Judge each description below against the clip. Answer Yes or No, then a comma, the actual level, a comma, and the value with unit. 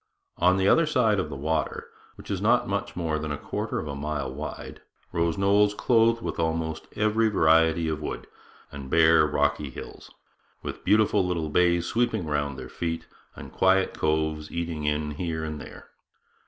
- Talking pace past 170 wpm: Yes, average, 180 wpm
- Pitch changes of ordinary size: Yes, average, 4.3 semitones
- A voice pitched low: Yes, very low, 80 Hz